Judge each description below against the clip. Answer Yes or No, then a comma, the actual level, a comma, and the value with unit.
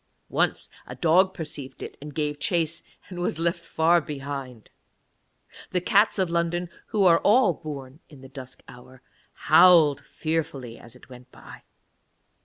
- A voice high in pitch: No, medium, 155 Hz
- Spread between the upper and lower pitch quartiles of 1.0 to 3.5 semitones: No, average, 4.4 semitones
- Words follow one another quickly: No, average, 150 wpm